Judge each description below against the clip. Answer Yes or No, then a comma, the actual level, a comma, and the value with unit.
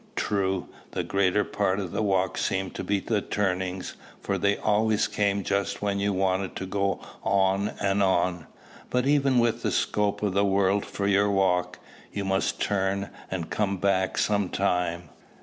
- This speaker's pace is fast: No, average, 170 wpm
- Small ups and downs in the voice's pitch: Yes, narrow, 1.4 semitones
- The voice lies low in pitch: Yes, low, 100 Hz